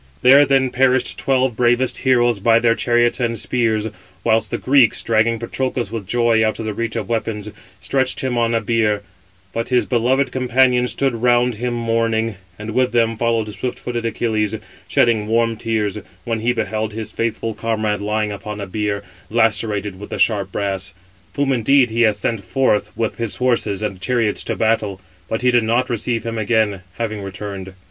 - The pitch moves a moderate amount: No, narrow, 2.2 semitones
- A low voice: Yes, low, 115 Hz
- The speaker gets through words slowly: No, average, 180 wpm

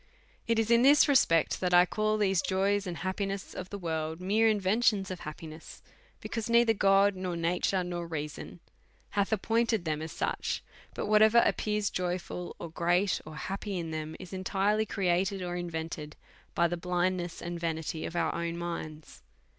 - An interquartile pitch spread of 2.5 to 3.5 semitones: Yes, average, 3.2 semitones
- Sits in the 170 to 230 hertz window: Yes, medium, 185 Hz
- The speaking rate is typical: Yes, average, 165 wpm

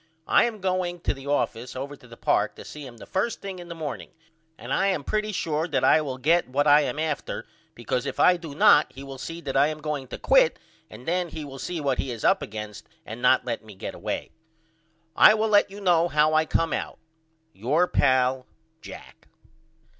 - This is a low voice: No, medium, 150 Hz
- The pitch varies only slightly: No, average, 5.0 semitones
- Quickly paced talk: Yes, fast, 220 wpm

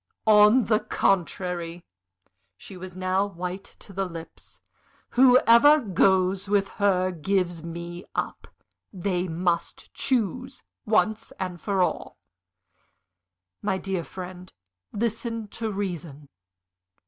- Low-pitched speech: No, high, 190 Hz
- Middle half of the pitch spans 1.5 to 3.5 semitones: Yes, average, 3.0 semitones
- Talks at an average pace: No, slow, 100 wpm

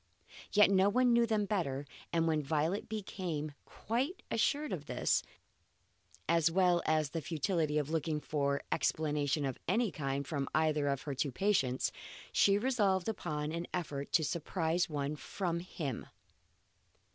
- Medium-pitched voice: Yes, medium, 165 Hz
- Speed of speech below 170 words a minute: Yes, average, 150 wpm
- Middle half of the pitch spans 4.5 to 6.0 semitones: Yes, average, 4.8 semitones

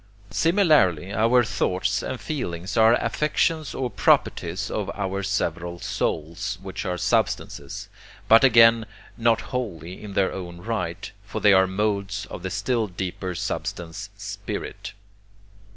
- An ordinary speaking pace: No, slow, 130 wpm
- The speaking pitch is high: No, low, 100 Hz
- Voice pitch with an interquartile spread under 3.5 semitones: No, average, 3.9 semitones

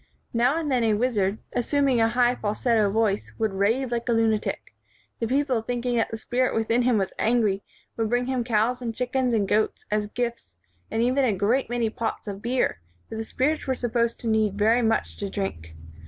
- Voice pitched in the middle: No, high, 230 Hz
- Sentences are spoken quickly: Yes, fast, 210 wpm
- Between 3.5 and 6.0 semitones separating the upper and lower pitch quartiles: No, narrow, 2.5 semitones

